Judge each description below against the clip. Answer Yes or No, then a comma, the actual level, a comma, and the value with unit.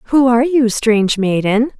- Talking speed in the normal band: Yes, average, 165 wpm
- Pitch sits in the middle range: No, high, 235 Hz